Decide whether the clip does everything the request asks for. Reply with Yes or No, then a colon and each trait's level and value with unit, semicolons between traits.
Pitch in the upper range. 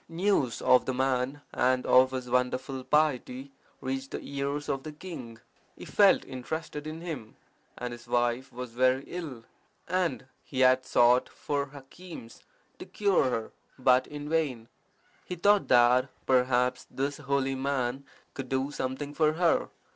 No: low, 135 Hz